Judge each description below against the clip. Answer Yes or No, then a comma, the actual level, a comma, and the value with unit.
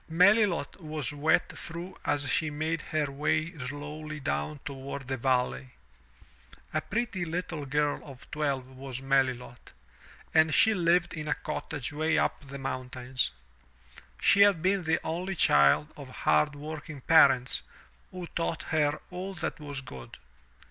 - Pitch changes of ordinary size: Yes, average, 3.6 semitones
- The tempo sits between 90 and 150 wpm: Yes, average, 140 wpm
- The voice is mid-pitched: Yes, medium, 150 Hz